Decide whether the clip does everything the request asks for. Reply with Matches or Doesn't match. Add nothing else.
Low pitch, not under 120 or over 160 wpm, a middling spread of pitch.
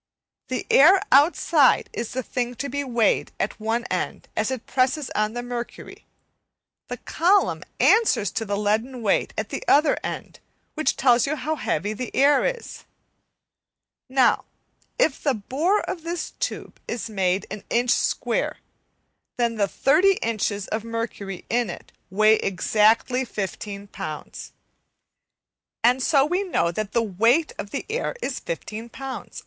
Doesn't match